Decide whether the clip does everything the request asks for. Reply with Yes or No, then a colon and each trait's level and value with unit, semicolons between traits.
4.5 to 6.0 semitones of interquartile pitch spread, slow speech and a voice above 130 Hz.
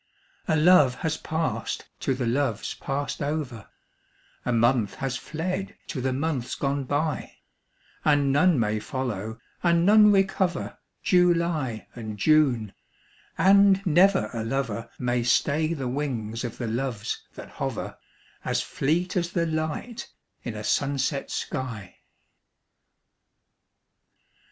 Yes: wide, 5.6 semitones; slow, 120 wpm; medium, 140 Hz